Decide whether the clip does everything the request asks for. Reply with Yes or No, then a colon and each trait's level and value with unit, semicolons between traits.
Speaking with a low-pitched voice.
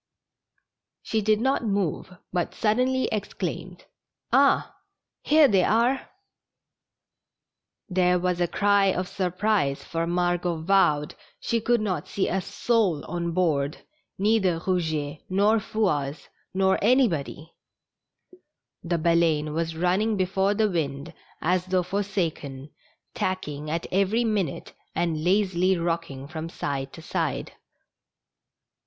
No: medium, 180 Hz